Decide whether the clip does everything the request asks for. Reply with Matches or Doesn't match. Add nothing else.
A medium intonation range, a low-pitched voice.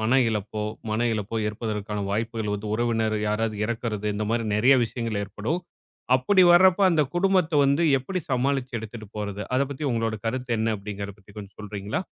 Matches